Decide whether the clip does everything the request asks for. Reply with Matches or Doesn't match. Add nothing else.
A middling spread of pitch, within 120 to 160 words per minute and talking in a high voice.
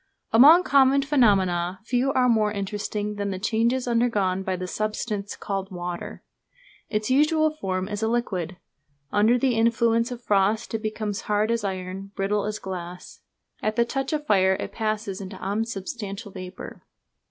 Matches